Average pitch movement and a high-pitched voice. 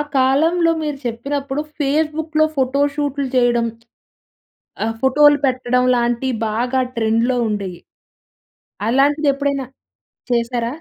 Yes: average, 3.2 semitones; very high, 265 Hz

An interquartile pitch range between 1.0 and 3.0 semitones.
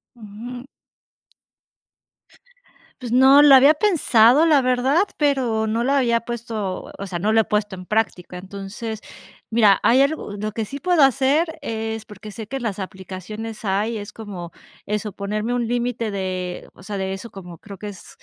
No: average, 3.9 semitones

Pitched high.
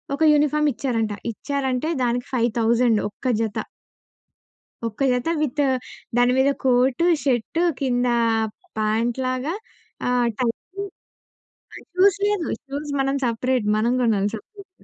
Yes: very high, 250 Hz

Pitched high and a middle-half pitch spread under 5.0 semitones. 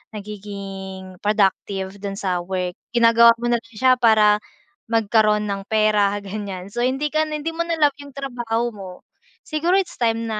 Yes: high, 215 Hz; average, 3.7 semitones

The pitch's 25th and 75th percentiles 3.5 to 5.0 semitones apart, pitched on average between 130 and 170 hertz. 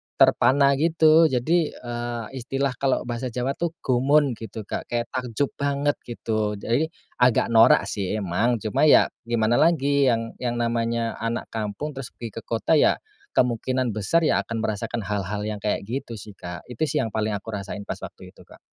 No: average, 3.9 semitones; low, 120 Hz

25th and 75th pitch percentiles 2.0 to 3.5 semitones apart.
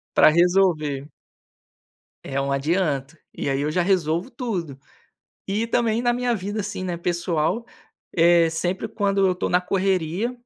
No: average, 4.1 semitones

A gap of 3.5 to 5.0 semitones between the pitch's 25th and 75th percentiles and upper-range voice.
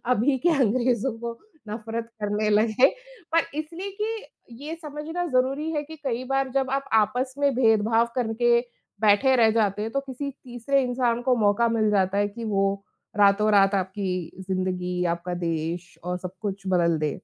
Yes: average, 4.7 semitones; high, 230 Hz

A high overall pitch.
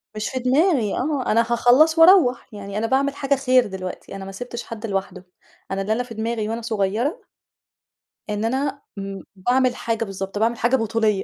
Yes: high, 230 Hz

